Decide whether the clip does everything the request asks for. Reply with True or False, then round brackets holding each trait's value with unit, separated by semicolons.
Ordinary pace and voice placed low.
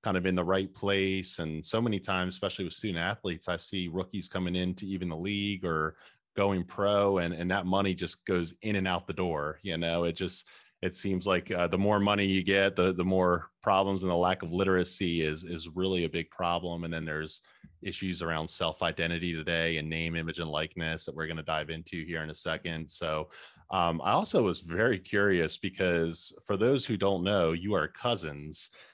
False (215 wpm; 90 Hz)